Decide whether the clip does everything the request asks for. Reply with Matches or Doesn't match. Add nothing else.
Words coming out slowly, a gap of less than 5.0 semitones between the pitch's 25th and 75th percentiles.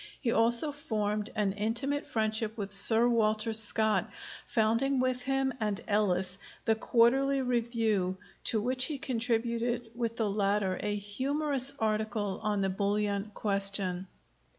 Matches